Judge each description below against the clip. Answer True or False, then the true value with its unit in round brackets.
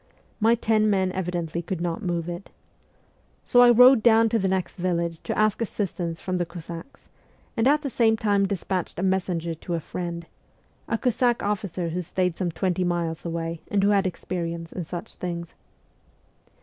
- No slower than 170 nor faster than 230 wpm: True (175 wpm)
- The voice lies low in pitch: False (185 Hz)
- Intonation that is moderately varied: True (3.9 semitones)